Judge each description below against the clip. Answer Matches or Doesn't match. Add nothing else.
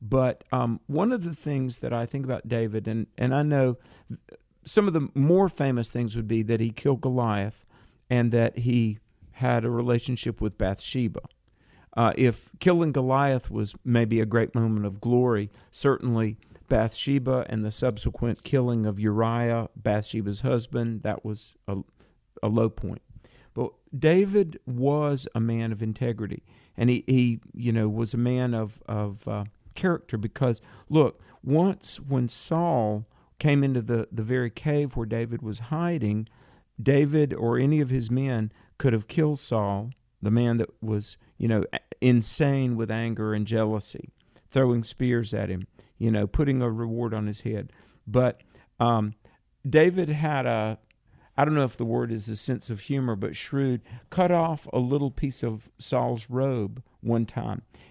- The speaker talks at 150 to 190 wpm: Matches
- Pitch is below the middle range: Matches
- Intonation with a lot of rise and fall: Doesn't match